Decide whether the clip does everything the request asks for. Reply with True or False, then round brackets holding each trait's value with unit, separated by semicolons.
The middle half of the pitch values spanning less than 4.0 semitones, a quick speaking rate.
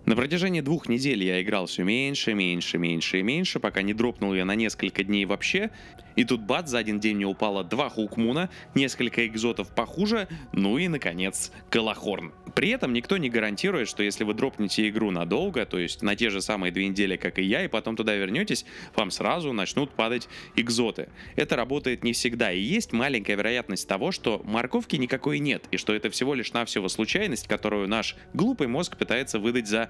False (4.4 semitones; 190 wpm)